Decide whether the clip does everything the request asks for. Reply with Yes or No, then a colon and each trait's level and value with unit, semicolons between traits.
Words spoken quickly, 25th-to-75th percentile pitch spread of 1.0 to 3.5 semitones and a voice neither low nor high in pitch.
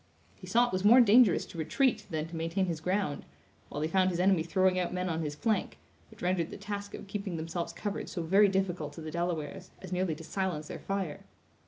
Yes: fast, 225 wpm; average, 3.2 semitones; medium, 180 Hz